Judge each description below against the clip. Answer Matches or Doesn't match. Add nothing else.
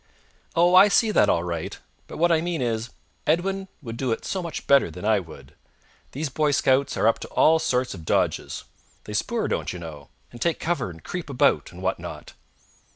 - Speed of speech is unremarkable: Doesn't match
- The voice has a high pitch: Doesn't match